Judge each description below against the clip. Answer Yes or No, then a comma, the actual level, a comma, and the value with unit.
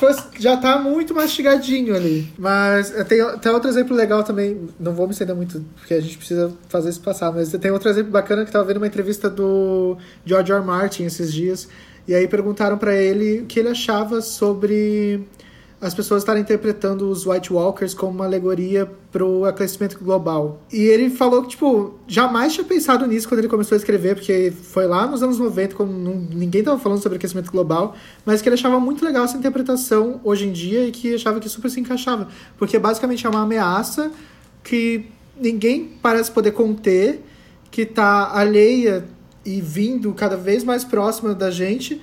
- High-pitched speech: Yes, high, 210 Hz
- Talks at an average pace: No, fast, 190 wpm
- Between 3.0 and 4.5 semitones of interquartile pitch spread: Yes, average, 3.4 semitones